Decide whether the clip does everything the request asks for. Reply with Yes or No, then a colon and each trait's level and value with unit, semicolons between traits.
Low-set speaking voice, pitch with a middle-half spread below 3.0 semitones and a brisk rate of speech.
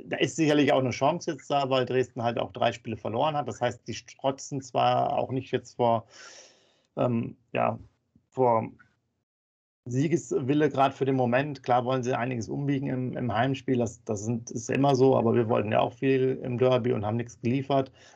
Yes: low, 125 Hz; narrow, 2.4 semitones; fast, 195 wpm